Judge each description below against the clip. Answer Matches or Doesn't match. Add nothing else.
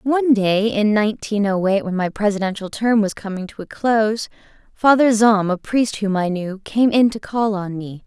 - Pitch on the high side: Matches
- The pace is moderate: Doesn't match